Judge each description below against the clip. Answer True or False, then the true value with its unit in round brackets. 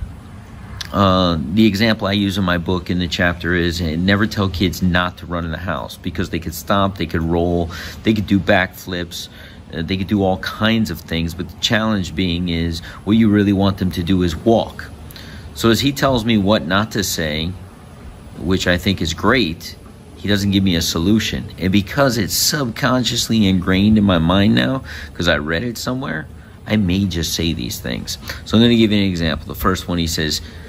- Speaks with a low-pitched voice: True (95 Hz)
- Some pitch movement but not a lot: True (3.6 semitones)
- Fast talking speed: True (210 wpm)